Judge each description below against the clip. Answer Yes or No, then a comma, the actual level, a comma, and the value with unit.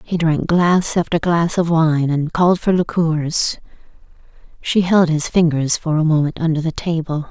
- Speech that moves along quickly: No, average, 170 wpm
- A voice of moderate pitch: Yes, medium, 165 Hz